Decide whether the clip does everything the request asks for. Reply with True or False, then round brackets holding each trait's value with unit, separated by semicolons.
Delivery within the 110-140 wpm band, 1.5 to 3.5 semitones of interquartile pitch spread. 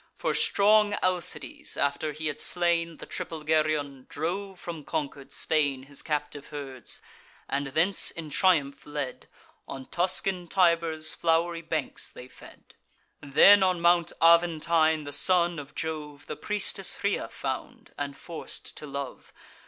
True (135 wpm; 3.2 semitones)